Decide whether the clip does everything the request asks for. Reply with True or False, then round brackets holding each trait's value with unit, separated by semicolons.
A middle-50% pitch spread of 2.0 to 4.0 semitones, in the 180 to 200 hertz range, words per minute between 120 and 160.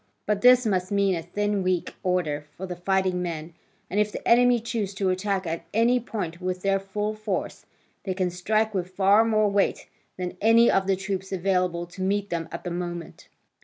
False (2.5 semitones; 190 Hz; 200 wpm)